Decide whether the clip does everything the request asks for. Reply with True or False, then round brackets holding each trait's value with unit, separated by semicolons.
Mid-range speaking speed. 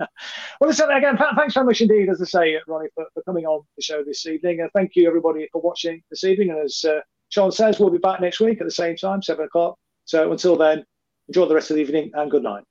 False (260 wpm)